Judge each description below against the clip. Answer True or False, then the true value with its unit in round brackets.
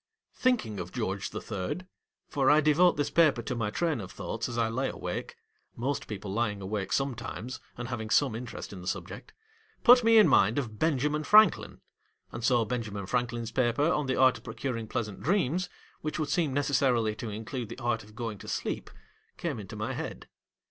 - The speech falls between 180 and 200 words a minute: True (195 wpm)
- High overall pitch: False (120 Hz)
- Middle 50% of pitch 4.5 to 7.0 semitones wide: True (4.9 semitones)